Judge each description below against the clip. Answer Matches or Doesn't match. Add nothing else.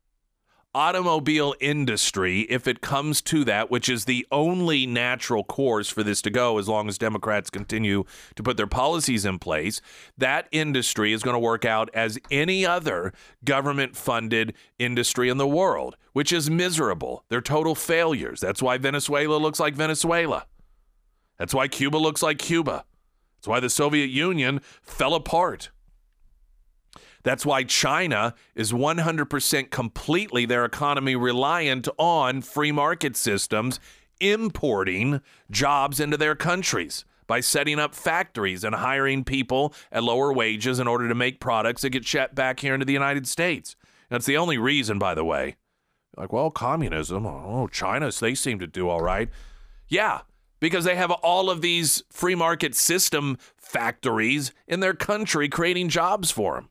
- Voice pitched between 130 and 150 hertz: Matches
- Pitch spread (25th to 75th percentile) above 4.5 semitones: Matches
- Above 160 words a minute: Doesn't match